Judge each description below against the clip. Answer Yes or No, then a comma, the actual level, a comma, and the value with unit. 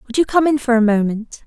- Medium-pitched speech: No, high, 245 Hz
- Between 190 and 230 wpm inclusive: No, fast, 285 wpm